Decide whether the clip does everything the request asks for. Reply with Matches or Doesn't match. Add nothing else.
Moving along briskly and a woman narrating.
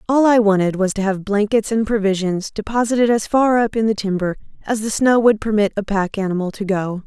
Matches